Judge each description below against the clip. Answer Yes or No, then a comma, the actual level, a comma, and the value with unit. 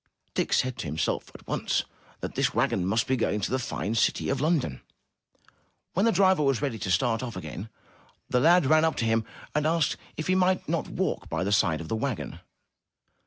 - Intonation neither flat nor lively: No, wide, 7.3 semitones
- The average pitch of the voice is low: Yes, low, 125 Hz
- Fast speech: Yes, fast, 210 wpm